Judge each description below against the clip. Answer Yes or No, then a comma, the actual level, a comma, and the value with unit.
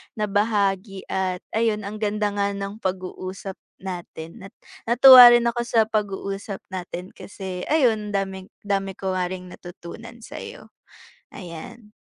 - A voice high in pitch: Yes, high, 200 Hz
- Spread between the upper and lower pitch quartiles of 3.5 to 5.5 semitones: No, narrow, 2.4 semitones